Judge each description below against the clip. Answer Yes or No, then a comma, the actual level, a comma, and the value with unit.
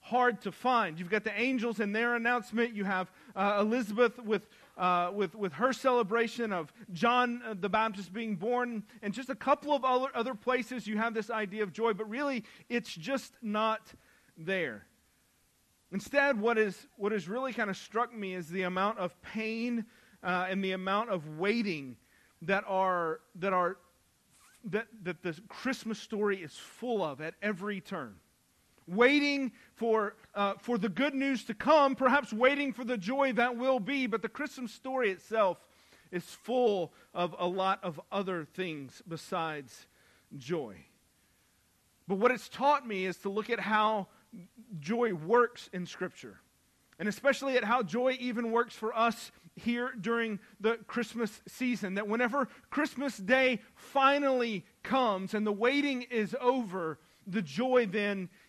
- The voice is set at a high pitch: Yes, high, 220 Hz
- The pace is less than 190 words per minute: Yes, average, 160 wpm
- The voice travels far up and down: No, average, 4.6 semitones